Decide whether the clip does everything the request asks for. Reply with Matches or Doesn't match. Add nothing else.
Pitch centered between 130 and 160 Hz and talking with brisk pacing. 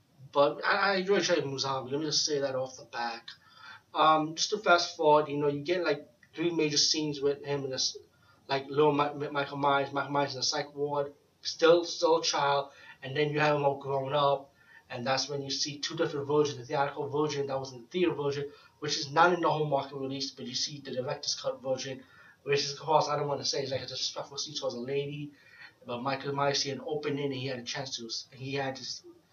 Matches